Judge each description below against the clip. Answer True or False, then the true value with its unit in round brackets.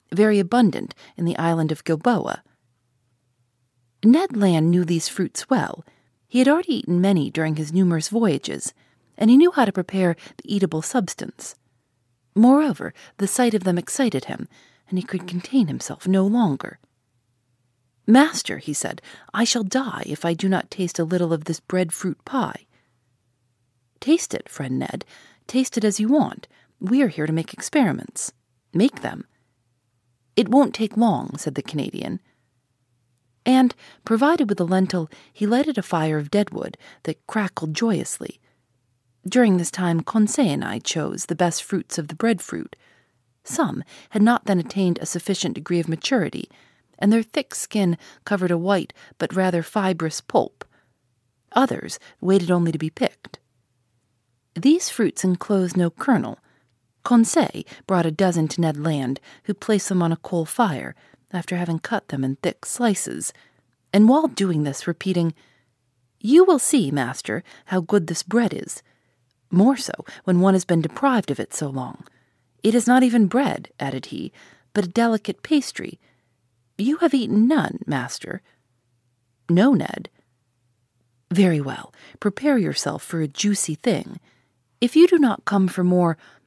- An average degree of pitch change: False (8.6 semitones)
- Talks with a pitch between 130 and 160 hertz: False (175 Hz)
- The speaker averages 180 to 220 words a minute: False (155 wpm)